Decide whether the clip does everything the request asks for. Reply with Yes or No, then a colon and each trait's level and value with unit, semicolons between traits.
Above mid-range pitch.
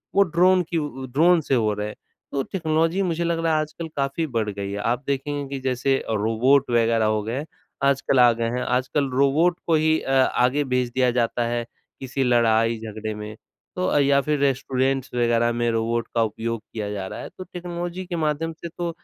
No: low, 130 Hz